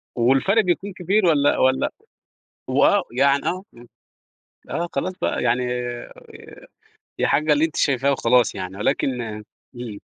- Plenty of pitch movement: Yes, wide, 5.8 semitones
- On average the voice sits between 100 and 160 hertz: Yes, medium, 140 Hz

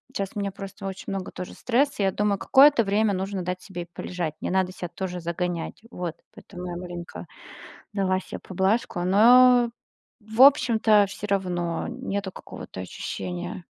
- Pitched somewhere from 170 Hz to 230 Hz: Yes, high, 190 Hz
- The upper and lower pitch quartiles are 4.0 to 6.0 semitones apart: No, average, 2.8 semitones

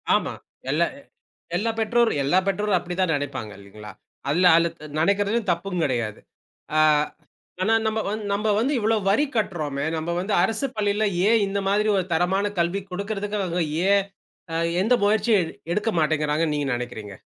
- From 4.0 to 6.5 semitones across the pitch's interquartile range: Yes, average, 5.1 semitones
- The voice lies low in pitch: No, high, 190 Hz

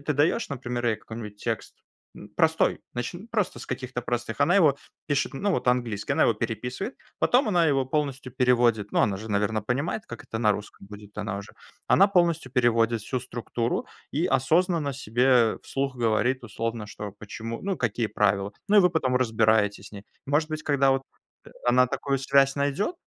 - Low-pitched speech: Yes, low, 125 Hz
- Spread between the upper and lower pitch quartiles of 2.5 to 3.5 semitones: No, average, 4.2 semitones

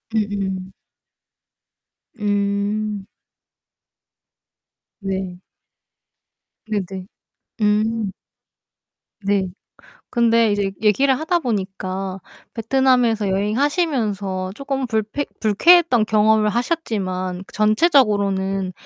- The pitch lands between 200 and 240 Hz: Yes, high, 210 Hz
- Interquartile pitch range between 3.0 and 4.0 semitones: Yes, average, 3.5 semitones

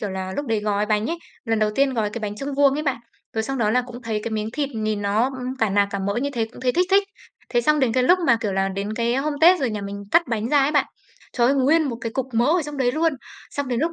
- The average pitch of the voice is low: No, high, 240 Hz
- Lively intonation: No, average, 4.7 semitones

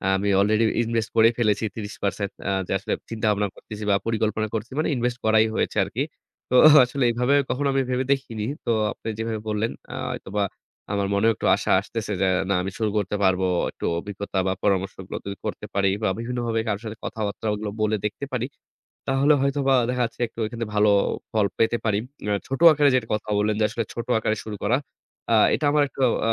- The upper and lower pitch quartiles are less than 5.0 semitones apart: Yes, narrow, 2.4 semitones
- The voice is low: Yes, low, 110 Hz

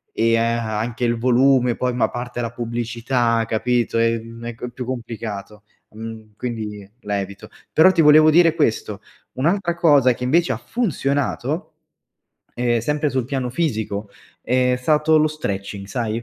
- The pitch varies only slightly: No, average, 3.3 semitones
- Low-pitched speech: Yes, low, 120 Hz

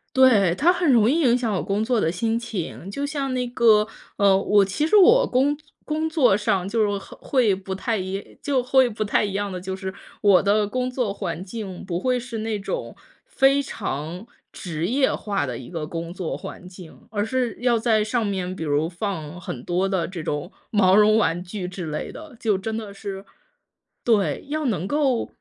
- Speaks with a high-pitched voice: Yes, high, 210 Hz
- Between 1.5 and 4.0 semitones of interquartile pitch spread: No, average, 5.0 semitones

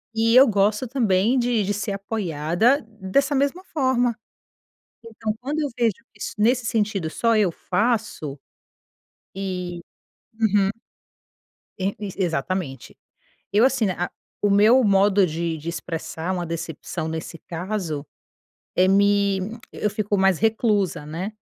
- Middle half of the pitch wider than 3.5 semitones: Yes, average, 4.1 semitones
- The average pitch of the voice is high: Yes, high, 200 Hz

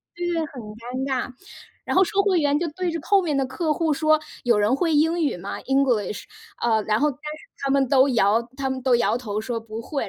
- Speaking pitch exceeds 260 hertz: Yes, very high, 270 Hz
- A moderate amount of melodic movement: Yes, average, 4.8 semitones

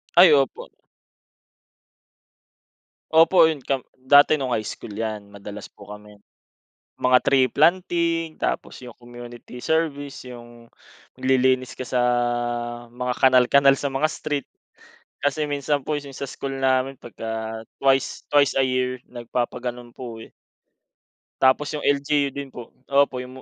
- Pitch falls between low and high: No, low, 130 Hz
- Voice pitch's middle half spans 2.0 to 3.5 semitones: Yes, average, 2.7 semitones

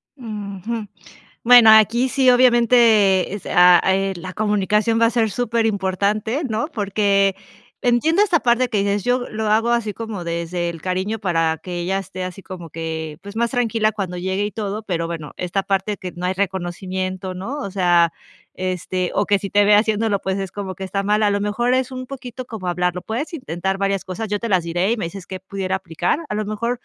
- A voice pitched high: Yes, high, 200 Hz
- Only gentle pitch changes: No, average, 3.5 semitones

